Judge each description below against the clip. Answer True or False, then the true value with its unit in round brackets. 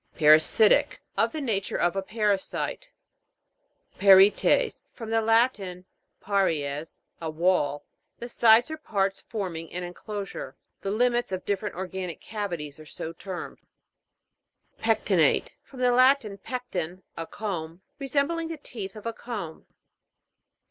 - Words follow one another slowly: True (130 wpm)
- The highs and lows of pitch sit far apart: False (4.7 semitones)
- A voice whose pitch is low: False (200 Hz)